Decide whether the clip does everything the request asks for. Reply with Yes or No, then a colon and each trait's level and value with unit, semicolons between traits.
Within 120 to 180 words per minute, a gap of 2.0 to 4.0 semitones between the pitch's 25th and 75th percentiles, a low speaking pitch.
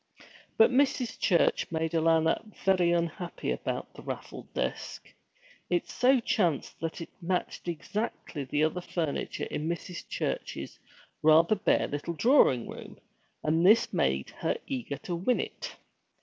No: slow, 135 wpm; average, 3.4 semitones; medium, 170 Hz